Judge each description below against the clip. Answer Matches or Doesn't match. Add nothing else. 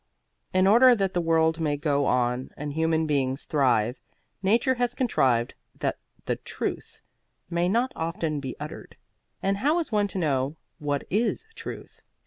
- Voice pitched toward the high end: Doesn't match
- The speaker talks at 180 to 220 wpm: Doesn't match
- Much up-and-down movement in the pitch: Matches